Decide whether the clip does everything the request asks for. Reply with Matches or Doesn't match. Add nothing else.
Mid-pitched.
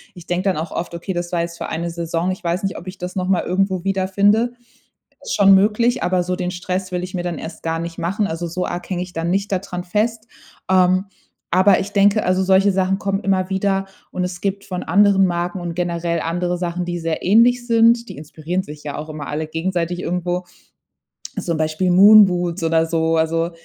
Matches